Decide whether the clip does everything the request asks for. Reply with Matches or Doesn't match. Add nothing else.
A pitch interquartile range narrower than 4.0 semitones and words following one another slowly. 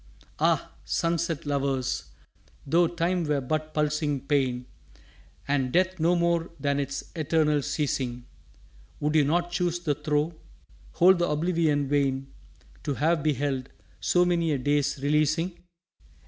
Matches